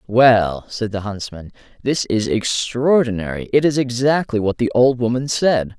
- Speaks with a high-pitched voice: No, low, 120 Hz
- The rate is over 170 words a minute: No, average, 155 wpm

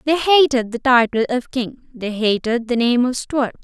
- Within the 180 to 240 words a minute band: Yes, average, 200 wpm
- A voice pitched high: Yes, high, 245 Hz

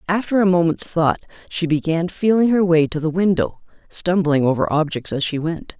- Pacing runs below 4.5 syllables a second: No, 5.2 syllables/s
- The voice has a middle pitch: Yes, medium, 170 Hz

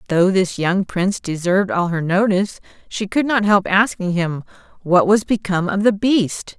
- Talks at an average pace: Yes, average, 180 wpm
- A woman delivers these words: Yes, female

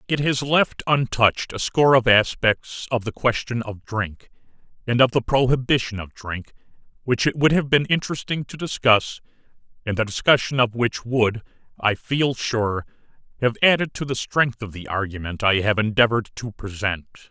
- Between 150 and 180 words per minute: Yes, average, 170 wpm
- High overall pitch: No, low, 120 Hz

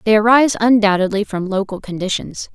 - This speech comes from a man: No, female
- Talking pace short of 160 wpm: Yes, average, 140 wpm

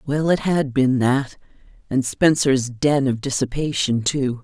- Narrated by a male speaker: No, female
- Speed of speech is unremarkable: Yes, average, 150 wpm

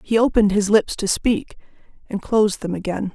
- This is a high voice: Yes, high, 210 Hz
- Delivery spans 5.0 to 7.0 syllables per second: Yes, 5.5 syllables/s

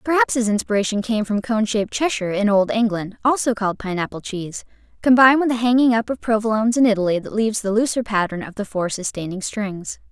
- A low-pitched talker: No, high, 220 Hz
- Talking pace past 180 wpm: Yes, average, 200 wpm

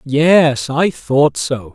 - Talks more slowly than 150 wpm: Yes, average, 140 wpm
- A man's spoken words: Yes, male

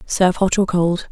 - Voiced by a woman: Yes, female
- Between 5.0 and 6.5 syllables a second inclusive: Yes, 5.2 syllables/s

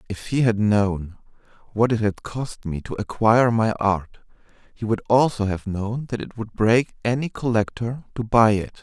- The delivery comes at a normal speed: Yes, average, 185 wpm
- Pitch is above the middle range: No, low, 110 Hz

